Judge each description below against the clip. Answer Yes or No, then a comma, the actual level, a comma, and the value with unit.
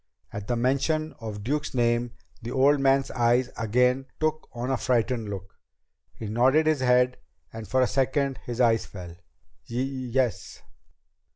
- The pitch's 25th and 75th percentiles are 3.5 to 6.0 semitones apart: No, narrow, 2.6 semitones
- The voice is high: No, low, 125 Hz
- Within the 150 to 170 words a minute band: Yes, average, 155 wpm